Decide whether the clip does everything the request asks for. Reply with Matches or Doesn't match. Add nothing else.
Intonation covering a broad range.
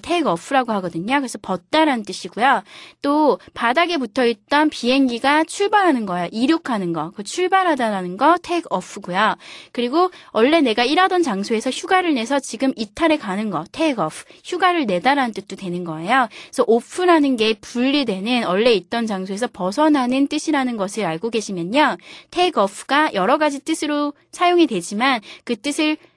Matches